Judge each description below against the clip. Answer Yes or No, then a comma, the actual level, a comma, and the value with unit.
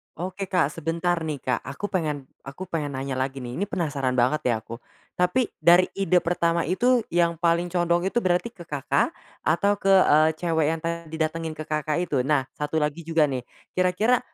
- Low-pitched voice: No, medium, 165 Hz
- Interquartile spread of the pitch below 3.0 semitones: No, average, 3.3 semitones